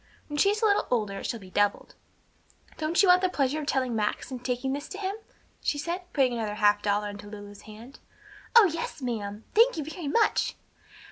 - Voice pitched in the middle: No, very high, 265 Hz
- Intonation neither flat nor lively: No, wide, 8.3 semitones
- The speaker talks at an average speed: No, fast, 210 wpm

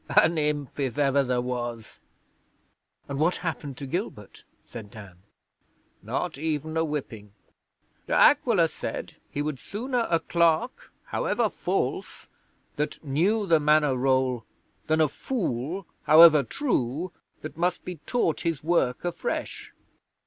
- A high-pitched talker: No, medium, 150 Hz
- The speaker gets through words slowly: Yes, slow, 130 wpm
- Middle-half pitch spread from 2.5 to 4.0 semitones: No, average, 4.5 semitones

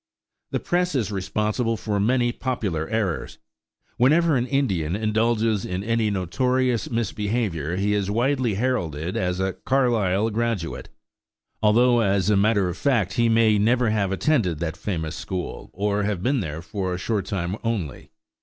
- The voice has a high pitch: No, low, 105 Hz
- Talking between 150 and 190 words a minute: Yes, average, 155 wpm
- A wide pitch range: No, average, 4.0 semitones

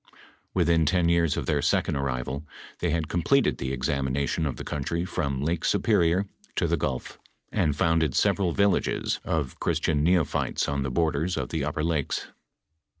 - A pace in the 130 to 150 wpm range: No, average, 165 wpm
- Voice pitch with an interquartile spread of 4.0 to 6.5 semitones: No, average, 3.3 semitones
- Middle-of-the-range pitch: No, very low, 80 Hz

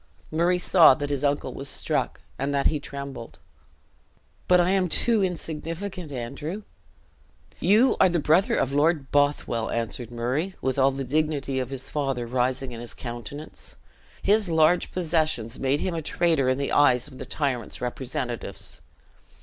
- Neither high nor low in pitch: Yes, medium, 145 Hz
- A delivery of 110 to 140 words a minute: No, average, 160 wpm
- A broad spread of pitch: No, average, 4.4 semitones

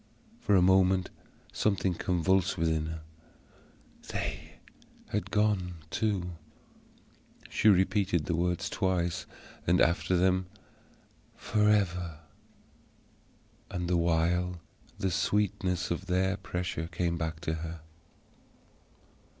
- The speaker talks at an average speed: No, slow, 100 wpm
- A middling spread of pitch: No, narrow, 1.9 semitones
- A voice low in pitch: Yes, very low, 90 Hz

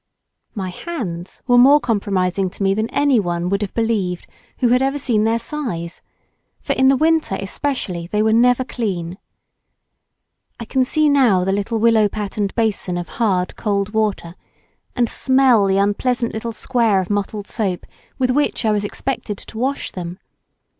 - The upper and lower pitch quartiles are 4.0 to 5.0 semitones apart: Yes, average, 4.4 semitones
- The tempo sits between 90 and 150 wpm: No, average, 165 wpm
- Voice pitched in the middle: No, high, 215 Hz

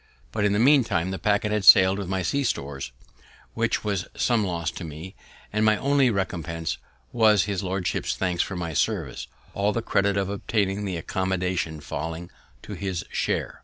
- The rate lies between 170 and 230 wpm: Yes, average, 175 wpm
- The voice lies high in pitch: No, very low, 95 Hz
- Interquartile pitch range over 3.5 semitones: No, average, 3.1 semitones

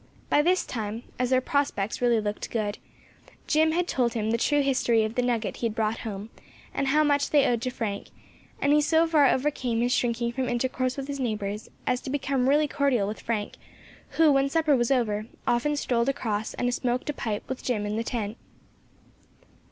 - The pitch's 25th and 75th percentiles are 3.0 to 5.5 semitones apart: Yes, average, 3.9 semitones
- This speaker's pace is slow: No, average, 200 wpm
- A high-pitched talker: Yes, high, 245 Hz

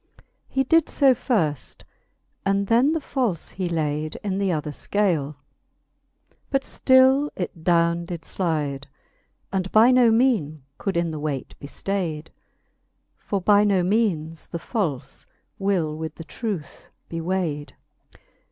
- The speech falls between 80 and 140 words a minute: Yes, slow, 135 wpm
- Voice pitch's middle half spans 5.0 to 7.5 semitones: Yes, wide, 5.6 semitones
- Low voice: No, medium, 180 Hz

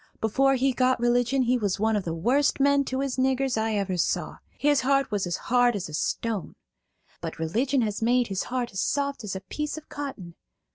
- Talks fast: Yes, fast, 210 wpm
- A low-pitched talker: No, high, 245 Hz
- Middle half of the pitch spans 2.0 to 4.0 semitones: No, average, 4.8 semitones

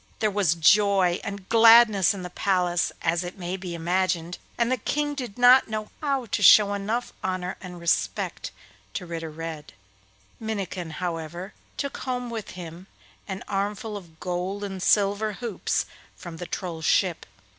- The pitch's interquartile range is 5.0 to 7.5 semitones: No, average, 3.6 semitones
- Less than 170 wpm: Yes, average, 155 wpm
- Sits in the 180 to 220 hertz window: Yes, high, 190 Hz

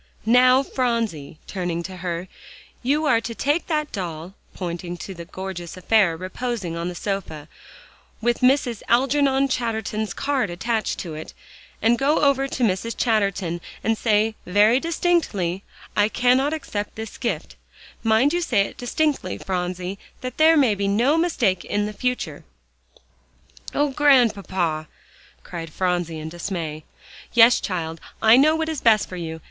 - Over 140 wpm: Yes, average, 150 wpm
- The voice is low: No, high, 215 Hz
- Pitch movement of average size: No, wide, 6.1 semitones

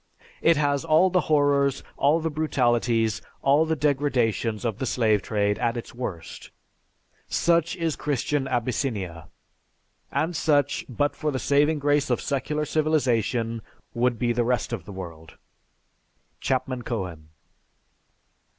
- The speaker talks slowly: Yes, slow, 130 wpm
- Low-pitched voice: Yes, low, 130 Hz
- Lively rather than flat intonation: No, average, 4.5 semitones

